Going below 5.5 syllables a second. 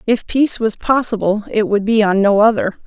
Yes: 5.3 syllables/s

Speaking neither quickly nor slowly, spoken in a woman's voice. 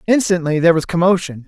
No: average, 165 wpm; male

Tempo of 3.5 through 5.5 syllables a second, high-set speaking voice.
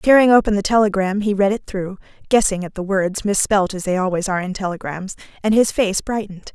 No: 5.9 syllables/s; high, 200 Hz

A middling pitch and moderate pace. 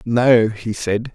No: low, 115 Hz; average, 155 wpm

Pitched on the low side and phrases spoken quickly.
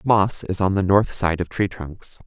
Yes: very low, 95 Hz; fast, 240 wpm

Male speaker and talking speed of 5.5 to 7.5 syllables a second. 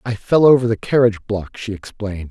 Yes: male; 5.9 syllables/s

